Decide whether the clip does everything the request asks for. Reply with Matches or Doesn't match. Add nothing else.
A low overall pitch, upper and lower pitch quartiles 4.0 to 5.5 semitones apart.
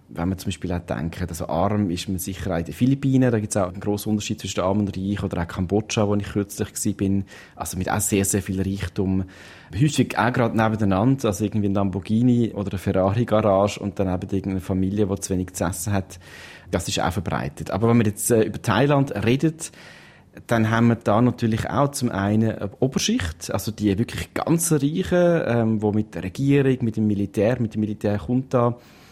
Doesn't match